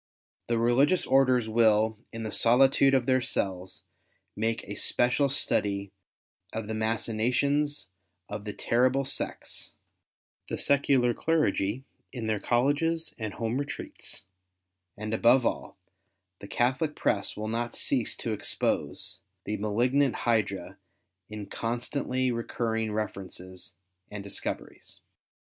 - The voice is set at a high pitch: No, low, 115 Hz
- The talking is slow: Yes, slow, 120 wpm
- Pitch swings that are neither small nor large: Yes, average, 3.5 semitones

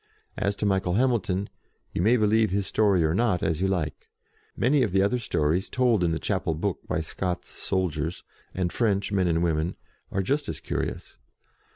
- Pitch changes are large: No, average, 3.6 semitones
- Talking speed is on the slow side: No, average, 190 wpm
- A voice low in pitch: Yes, very low, 95 Hz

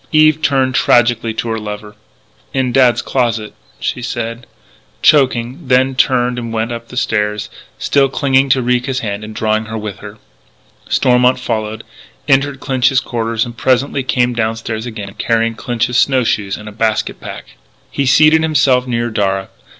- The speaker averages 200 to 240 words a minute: No, average, 160 wpm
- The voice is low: Yes, low, 120 Hz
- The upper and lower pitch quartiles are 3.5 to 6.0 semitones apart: No, average, 2.8 semitones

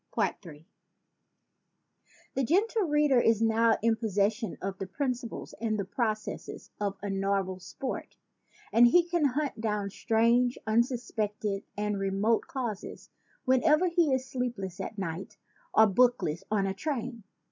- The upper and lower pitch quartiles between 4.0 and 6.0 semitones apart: Yes, average, 4.4 semitones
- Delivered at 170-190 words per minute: No, slow, 135 wpm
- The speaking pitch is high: Yes, high, 225 Hz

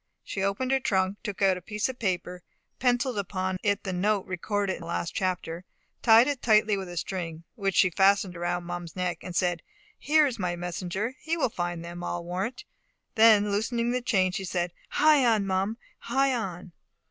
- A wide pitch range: No, average, 4.2 semitones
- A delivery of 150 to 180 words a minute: No, average, 195 wpm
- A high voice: Yes, high, 195 Hz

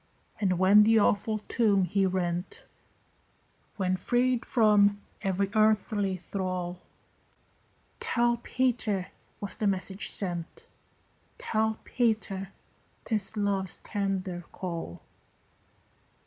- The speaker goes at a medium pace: No, slow, 90 wpm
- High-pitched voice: Yes, high, 200 Hz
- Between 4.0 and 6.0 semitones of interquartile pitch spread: No, average, 2.7 semitones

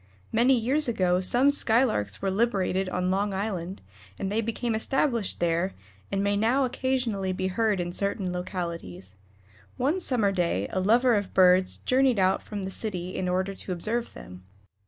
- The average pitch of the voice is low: No, high, 195 Hz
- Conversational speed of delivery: Yes, average, 165 wpm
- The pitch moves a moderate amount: Yes, average, 4.2 semitones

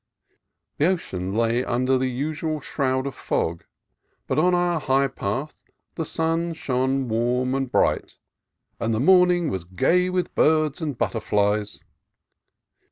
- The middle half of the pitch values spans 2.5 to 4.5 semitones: No, average, 5.3 semitones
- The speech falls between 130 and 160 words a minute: Yes, average, 140 wpm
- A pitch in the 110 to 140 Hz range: Yes, low, 135 Hz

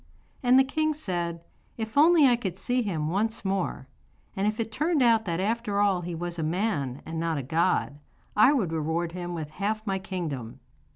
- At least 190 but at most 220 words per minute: Yes, average, 195 wpm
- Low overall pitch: No, high, 190 Hz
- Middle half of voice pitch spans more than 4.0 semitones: Yes, average, 5.3 semitones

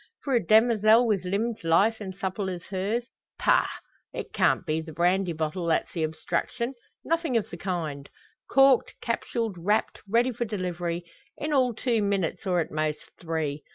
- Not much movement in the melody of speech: No, average, 5.3 semitones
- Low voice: No, high, 195 Hz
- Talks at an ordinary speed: Yes, average, 165 wpm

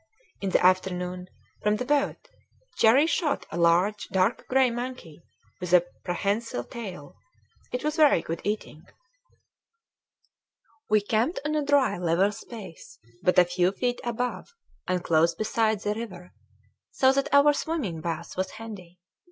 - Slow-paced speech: No, average, 145 wpm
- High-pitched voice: Yes, high, 205 Hz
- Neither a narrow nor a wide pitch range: No, wide, 5.7 semitones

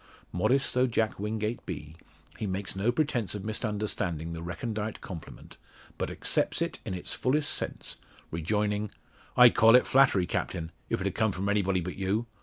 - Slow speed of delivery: No, average, 165 wpm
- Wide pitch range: No, average, 3.5 semitones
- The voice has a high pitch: No, low, 105 Hz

